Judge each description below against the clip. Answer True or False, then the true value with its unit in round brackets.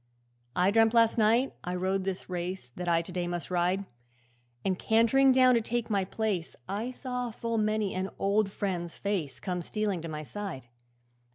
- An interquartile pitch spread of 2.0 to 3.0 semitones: False (3.9 semitones)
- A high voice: True (195 Hz)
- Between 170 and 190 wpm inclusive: True (180 wpm)